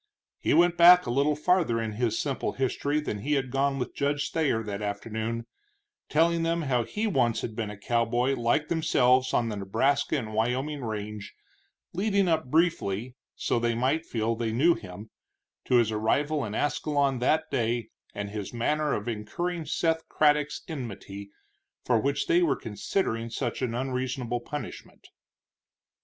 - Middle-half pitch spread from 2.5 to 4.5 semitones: No, average, 5.1 semitones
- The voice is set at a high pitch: No, low, 125 Hz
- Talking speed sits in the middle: Yes, average, 160 wpm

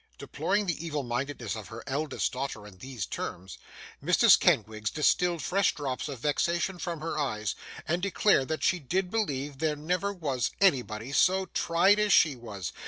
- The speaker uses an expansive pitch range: Yes, wide, 6.2 semitones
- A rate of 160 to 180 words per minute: Yes, average, 170 wpm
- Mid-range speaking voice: Yes, medium, 150 Hz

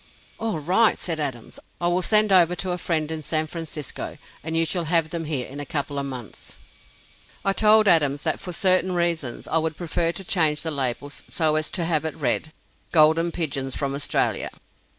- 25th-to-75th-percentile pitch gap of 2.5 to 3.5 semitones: Yes, average, 3.0 semitones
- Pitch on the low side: No, medium, 160 Hz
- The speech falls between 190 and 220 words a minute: Yes, average, 195 wpm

